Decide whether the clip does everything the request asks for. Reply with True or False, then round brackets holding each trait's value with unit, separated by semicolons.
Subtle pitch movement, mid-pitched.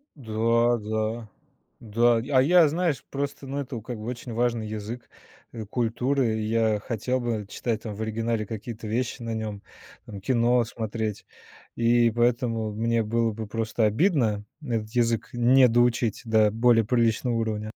False (1.8 semitones; 115 Hz)